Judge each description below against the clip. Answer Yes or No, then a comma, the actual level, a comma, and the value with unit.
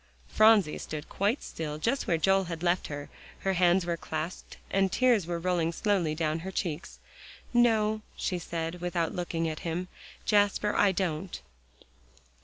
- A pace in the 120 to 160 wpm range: Yes, average, 155 wpm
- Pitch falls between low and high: Yes, medium, 175 Hz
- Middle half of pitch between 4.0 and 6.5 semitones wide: No, average, 3.4 semitones